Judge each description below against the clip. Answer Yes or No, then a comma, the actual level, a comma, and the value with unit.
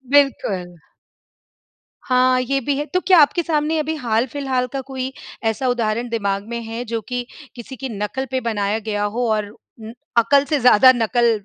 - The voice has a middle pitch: No, high, 245 Hz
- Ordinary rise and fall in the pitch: Yes, average, 3.4 semitones